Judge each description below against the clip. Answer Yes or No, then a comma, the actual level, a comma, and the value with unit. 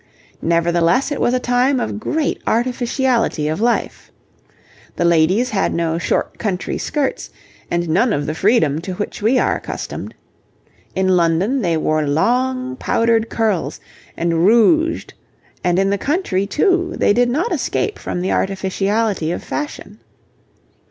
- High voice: Yes, high, 210 Hz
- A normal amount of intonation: No, wide, 6.6 semitones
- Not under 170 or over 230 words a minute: No, average, 145 wpm